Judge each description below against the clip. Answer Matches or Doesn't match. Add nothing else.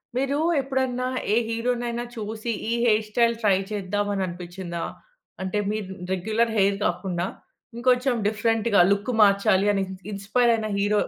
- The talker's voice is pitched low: Doesn't match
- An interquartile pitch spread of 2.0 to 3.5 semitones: Matches